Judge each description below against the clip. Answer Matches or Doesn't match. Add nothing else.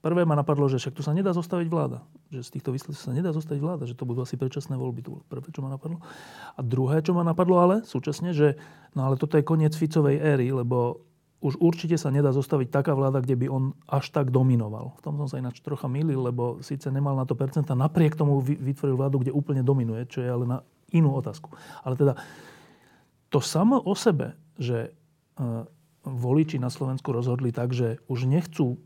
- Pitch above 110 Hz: Matches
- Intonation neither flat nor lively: Matches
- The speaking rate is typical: Doesn't match